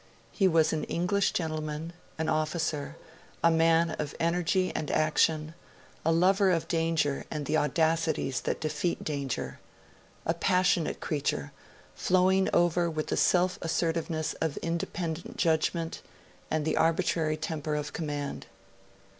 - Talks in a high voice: No, medium, 160 Hz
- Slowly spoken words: Yes, slow, 130 wpm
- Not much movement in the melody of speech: Yes, narrow, 1.7 semitones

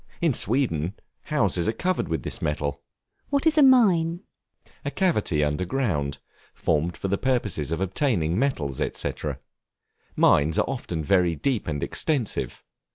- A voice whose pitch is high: No, low, 100 Hz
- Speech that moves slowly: No, average, 145 wpm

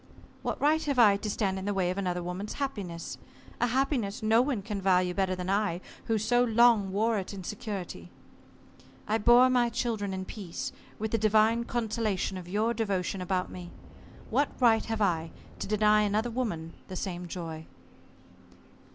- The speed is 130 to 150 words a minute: No, average, 175 wpm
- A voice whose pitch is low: No, high, 210 Hz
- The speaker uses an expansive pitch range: No, average, 3.7 semitones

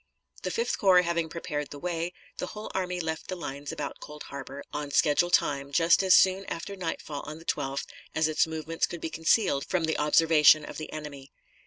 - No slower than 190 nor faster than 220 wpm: Yes, average, 200 wpm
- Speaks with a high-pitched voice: No, medium, 160 Hz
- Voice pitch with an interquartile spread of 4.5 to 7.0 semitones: No, average, 2.9 semitones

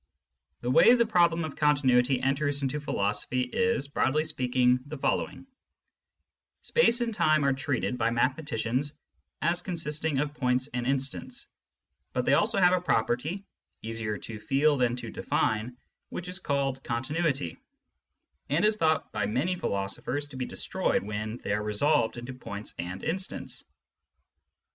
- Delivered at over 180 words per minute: No, average, 150 wpm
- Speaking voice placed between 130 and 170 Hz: Yes, low, 135 Hz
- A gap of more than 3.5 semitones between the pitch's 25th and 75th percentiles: Yes, average, 4.6 semitones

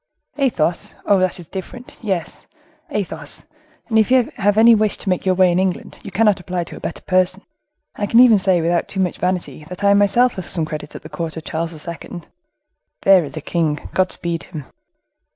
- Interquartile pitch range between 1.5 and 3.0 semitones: No, average, 3.5 semitones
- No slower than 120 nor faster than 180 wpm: No, average, 195 wpm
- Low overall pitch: No, medium, 185 Hz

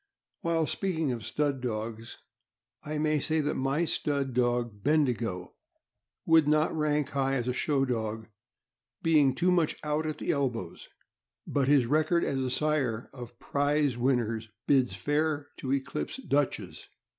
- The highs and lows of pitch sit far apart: No, average, 3.8 semitones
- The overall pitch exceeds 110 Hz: Yes, medium, 140 Hz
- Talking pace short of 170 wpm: Yes, average, 145 wpm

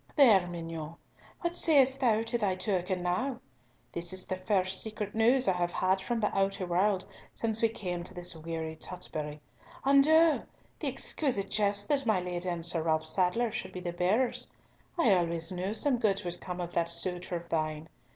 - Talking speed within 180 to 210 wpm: Yes, average, 190 wpm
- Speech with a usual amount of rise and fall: Yes, average, 4.3 semitones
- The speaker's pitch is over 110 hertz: Yes, medium, 185 Hz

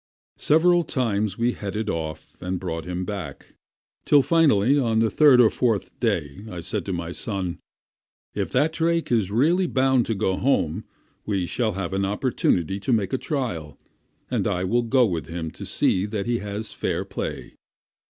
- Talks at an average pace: Yes, average, 180 wpm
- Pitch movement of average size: No, wide, 5.8 semitones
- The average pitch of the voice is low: Yes, low, 105 Hz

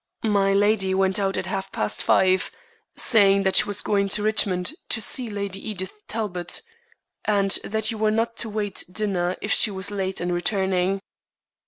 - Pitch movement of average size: No, narrow, 2.0 semitones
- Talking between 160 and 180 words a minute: Yes, average, 170 wpm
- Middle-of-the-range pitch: No, high, 200 Hz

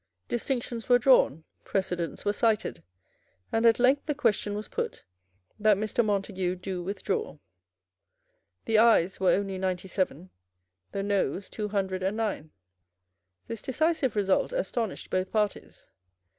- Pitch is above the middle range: Yes, high, 205 Hz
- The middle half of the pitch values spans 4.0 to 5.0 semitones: No, average, 3.4 semitones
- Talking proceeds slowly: Yes, slow, 130 wpm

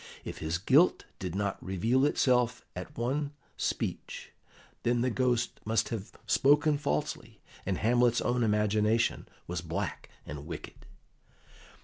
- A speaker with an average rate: No, slow, 125 wpm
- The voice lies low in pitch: Yes, low, 115 Hz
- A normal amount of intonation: Yes, average, 4.7 semitones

